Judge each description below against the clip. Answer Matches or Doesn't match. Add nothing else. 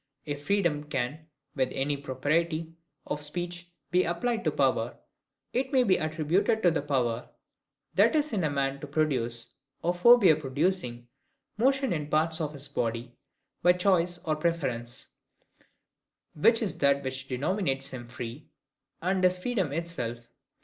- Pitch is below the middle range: Doesn't match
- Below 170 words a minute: Matches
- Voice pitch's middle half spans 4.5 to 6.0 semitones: Matches